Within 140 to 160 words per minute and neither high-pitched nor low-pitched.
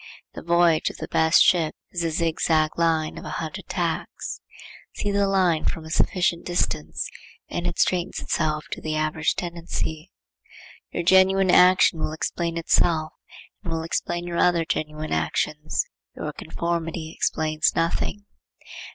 Yes: average, 145 wpm; medium, 165 Hz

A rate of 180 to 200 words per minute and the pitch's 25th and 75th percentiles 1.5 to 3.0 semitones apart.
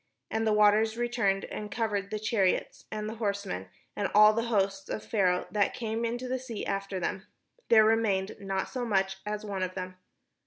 Yes: average, 190 wpm; narrow, 2.5 semitones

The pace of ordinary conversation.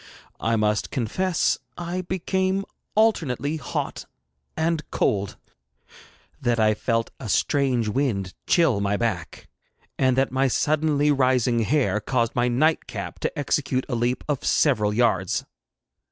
No: slow, 130 wpm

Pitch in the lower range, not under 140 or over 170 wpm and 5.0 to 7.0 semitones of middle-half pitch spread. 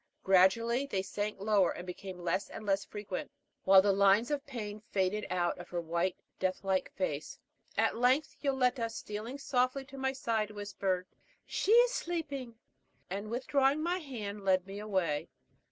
No: high, 210 Hz; average, 165 wpm; average, 5.3 semitones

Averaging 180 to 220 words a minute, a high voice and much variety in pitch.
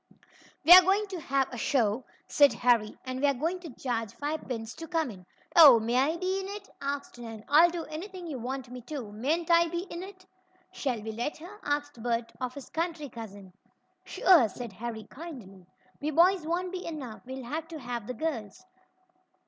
Yes: average, 195 wpm; very high, 280 Hz; wide, 6.1 semitones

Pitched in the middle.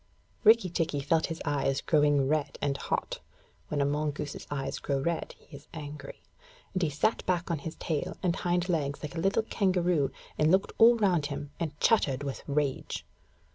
Yes: medium, 150 Hz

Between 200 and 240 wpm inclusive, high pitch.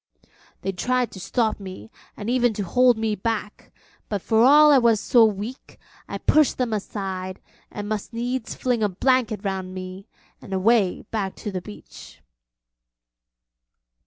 No: average, 155 wpm; high, 215 Hz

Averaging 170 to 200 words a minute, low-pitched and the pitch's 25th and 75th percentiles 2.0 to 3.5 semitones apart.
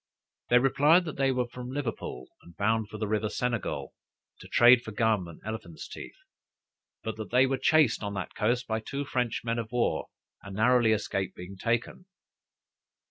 Yes: average, 180 wpm; low, 115 Hz; average, 2.9 semitones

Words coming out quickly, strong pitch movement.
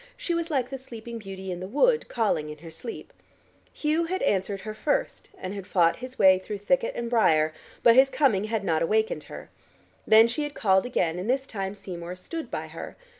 Yes: fast, 210 wpm; wide, 6.1 semitones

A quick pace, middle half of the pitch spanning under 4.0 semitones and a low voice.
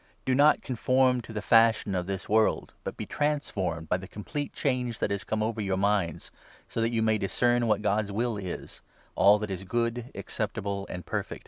Yes: fast, 215 wpm; average, 3.4 semitones; low, 110 Hz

